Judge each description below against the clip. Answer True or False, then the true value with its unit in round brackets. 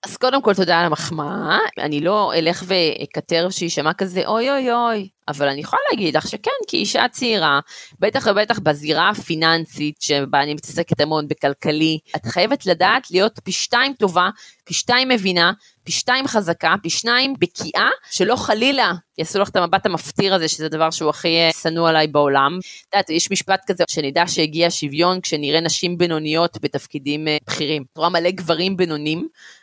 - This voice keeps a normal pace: False (165 wpm)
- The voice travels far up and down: False (4.1 semitones)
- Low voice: False (170 Hz)